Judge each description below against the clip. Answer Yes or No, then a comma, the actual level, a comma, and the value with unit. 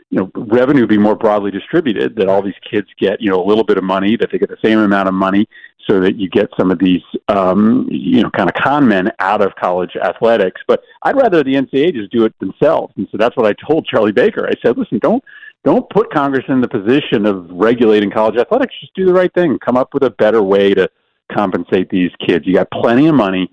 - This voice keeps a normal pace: No, fast, 245 wpm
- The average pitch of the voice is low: Yes, low, 120 Hz